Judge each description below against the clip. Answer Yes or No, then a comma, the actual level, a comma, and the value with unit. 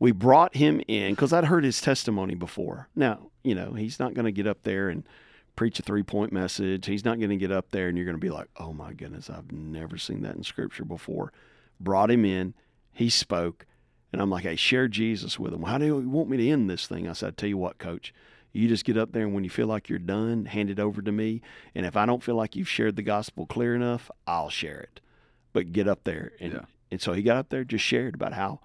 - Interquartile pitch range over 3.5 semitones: Yes, average, 3.9 semitones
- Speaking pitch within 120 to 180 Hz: No, low, 105 Hz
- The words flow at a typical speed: No, fast, 260 wpm